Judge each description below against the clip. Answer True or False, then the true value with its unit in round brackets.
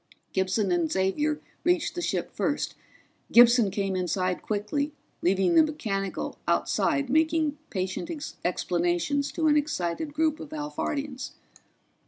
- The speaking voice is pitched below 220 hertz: False (245 Hz)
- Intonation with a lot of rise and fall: True (8.1 semitones)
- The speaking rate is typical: False (120 wpm)